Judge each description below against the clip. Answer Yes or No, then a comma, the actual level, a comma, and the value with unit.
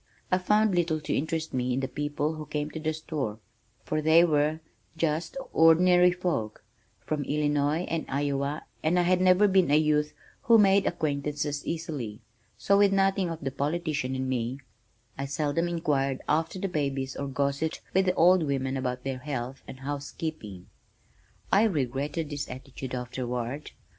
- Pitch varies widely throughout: No, average, 3.6 semitones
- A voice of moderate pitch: Yes, medium, 150 Hz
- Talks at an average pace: Yes, average, 165 wpm